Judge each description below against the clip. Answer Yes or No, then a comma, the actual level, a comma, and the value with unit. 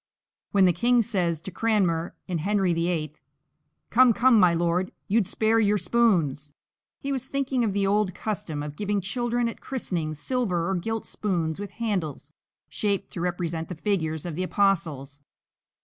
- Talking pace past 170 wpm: No, average, 165 wpm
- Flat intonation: No, average, 4.8 semitones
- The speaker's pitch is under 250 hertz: Yes, high, 190 Hz